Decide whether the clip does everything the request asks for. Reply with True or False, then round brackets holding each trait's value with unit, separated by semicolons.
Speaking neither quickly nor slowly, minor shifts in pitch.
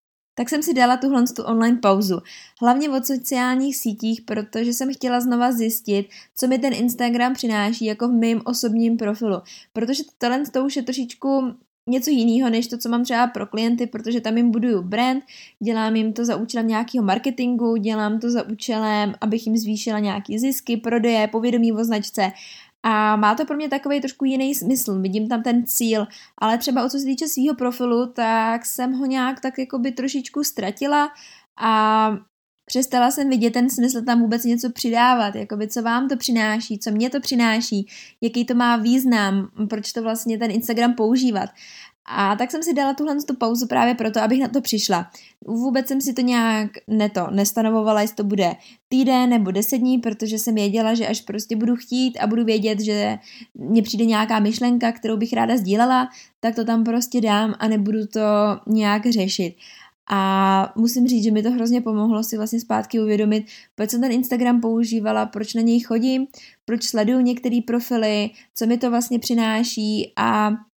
False (185 wpm; 2.3 semitones)